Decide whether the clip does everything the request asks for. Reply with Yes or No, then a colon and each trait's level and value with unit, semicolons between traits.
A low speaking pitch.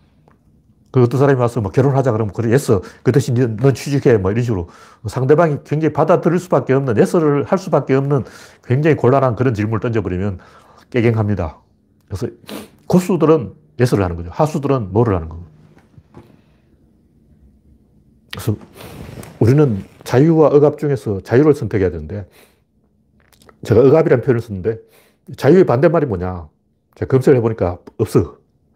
Yes: low, 125 Hz